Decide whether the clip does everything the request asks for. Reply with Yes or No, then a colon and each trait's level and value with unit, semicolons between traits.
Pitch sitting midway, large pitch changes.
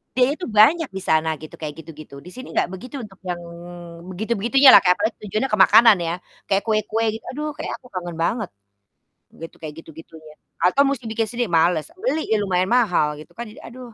No: high, 210 Hz; wide, 5.8 semitones